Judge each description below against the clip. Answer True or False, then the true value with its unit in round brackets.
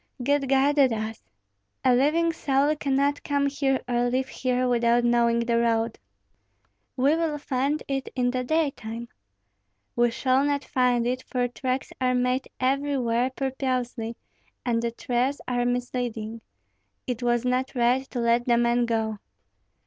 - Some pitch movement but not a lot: False (2.3 semitones)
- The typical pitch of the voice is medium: False (250 Hz)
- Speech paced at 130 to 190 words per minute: True (145 wpm)